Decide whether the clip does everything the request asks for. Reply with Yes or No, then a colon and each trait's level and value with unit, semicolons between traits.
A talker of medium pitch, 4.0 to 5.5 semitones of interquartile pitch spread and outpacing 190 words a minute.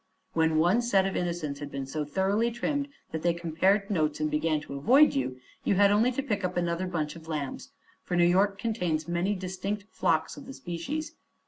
Yes: medium, 175 Hz; average, 4.5 semitones; fast, 205 wpm